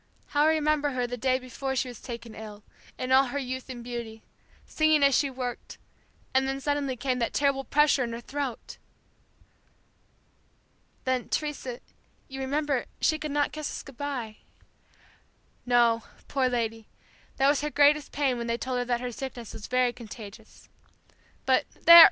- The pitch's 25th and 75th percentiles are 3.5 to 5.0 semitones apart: No, average, 3.0 semitones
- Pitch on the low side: No, very high, 260 Hz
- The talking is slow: No, average, 165 wpm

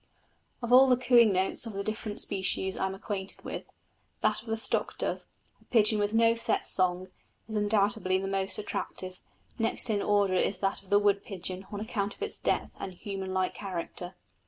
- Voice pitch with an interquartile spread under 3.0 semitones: Yes, narrow, 2.5 semitones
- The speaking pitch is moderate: No, high, 200 Hz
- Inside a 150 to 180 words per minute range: No, average, 195 wpm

